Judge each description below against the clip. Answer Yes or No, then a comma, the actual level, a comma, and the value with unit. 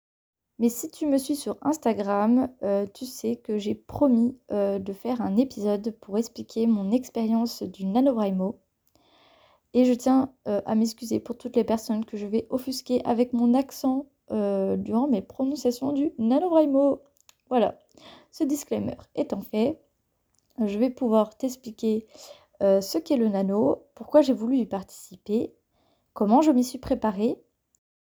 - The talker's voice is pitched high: Yes, high, 235 Hz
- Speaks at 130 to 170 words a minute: Yes, average, 150 wpm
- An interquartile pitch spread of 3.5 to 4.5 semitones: Yes, average, 3.8 semitones